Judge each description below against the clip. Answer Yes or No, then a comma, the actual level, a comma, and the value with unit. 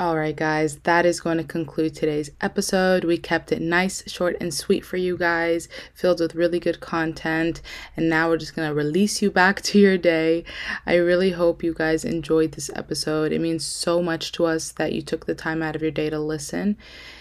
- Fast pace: Yes, fast, 215 wpm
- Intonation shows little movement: Yes, narrow, 1.8 semitones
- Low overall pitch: No, medium, 165 Hz